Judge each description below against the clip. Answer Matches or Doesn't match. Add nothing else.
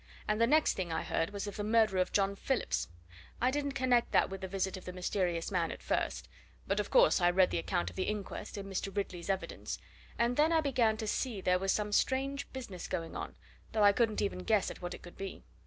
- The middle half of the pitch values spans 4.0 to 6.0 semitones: Matches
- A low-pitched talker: Doesn't match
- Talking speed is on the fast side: Matches